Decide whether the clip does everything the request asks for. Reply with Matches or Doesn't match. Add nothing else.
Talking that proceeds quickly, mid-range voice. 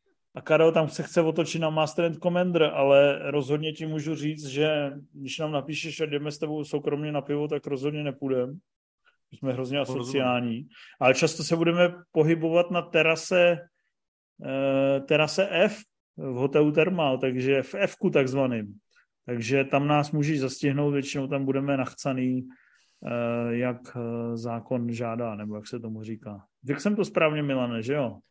Doesn't match